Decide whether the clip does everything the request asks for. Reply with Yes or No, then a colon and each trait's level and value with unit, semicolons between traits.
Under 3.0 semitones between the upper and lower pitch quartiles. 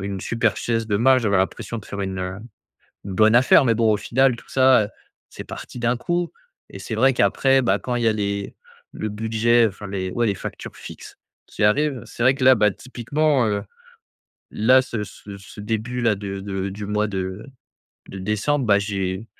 No: average, 3.3 semitones